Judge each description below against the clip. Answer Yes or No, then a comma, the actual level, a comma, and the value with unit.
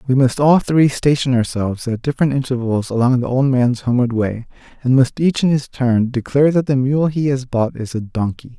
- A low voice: Yes, low, 130 Hz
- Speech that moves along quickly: Yes, fast, 215 wpm